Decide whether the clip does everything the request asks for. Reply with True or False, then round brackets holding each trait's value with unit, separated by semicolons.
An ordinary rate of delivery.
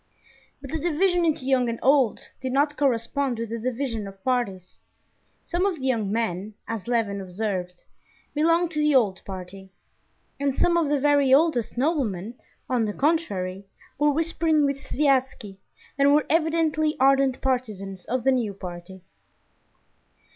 True (150 wpm)